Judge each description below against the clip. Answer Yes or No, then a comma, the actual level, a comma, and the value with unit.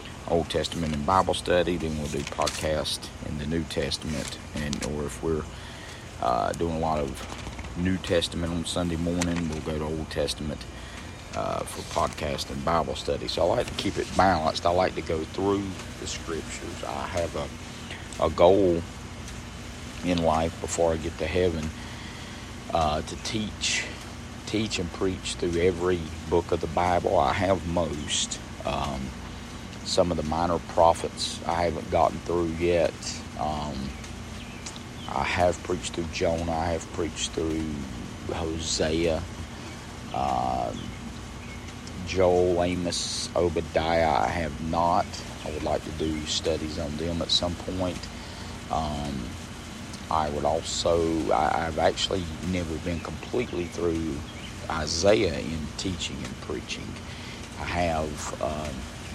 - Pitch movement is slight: Yes, narrow, 2.3 semitones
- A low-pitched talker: Yes, very low, 85 Hz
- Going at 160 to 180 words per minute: No, average, 140 wpm